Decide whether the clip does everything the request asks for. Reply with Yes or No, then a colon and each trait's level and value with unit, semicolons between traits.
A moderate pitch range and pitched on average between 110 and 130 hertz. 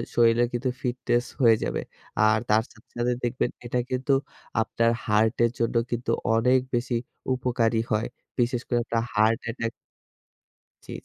No: narrow, 1.4 semitones; low, 120 Hz